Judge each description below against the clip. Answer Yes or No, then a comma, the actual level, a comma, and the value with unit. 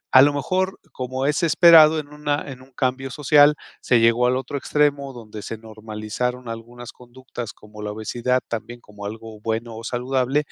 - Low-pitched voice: Yes, low, 125 Hz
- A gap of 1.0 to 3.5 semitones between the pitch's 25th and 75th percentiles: No, average, 4.0 semitones